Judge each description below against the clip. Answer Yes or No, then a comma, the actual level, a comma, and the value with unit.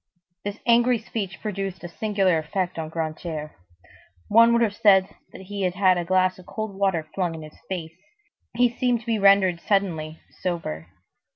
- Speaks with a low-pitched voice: No, high, 190 Hz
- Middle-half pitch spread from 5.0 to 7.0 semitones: No, average, 3.7 semitones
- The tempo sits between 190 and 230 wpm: No, average, 175 wpm